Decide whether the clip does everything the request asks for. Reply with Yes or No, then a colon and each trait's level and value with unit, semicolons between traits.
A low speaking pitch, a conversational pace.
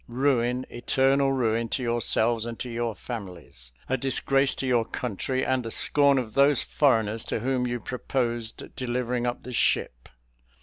Yes: low, 120 Hz; average, 160 wpm